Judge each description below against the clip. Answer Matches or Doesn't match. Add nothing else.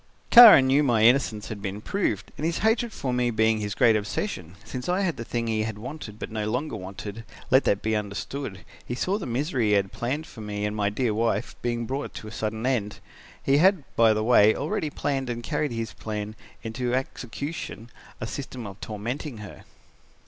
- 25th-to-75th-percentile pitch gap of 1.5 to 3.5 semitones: Doesn't match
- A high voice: Doesn't match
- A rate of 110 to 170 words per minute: Doesn't match